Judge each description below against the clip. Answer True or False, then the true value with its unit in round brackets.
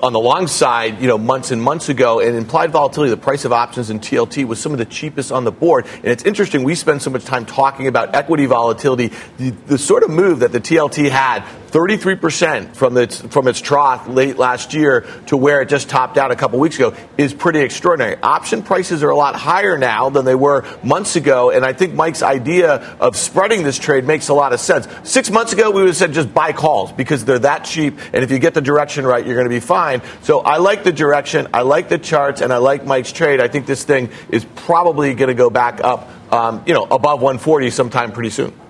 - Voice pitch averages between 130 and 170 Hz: True (140 Hz)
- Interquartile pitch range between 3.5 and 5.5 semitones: True (4.0 semitones)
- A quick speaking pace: True (240 wpm)